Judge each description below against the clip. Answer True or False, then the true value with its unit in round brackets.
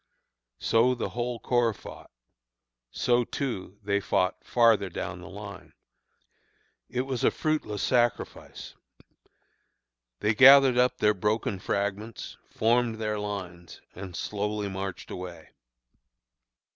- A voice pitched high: False (105 Hz)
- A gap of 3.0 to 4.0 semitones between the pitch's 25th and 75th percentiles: True (3.5 semitones)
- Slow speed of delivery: True (105 wpm)